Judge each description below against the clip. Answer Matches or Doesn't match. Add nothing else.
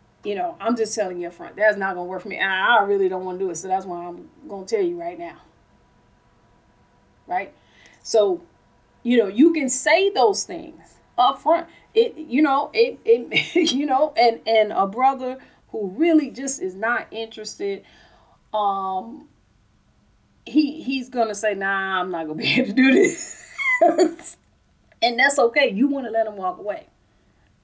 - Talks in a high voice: Matches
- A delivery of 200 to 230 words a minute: Doesn't match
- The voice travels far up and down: Matches